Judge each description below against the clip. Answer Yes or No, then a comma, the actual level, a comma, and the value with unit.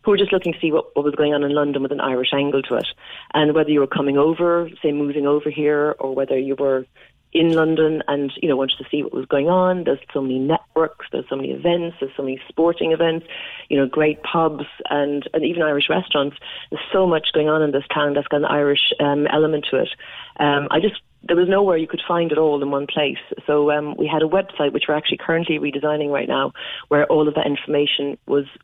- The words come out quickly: Yes, fast, 245 wpm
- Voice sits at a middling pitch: Yes, medium, 150 Hz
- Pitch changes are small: Yes, narrow, 2.2 semitones